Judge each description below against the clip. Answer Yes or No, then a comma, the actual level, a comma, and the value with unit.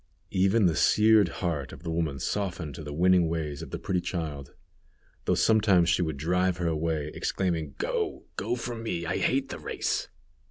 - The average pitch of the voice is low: Yes, very low, 85 Hz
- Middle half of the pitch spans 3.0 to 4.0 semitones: Yes, average, 3.4 semitones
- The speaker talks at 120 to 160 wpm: No, average, 185 wpm